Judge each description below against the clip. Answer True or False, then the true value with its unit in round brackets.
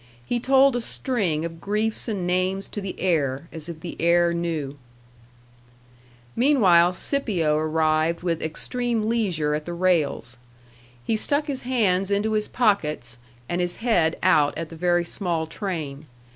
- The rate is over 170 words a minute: False (150 wpm)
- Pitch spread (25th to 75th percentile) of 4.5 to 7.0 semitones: True (5.1 semitones)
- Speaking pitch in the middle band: True (175 Hz)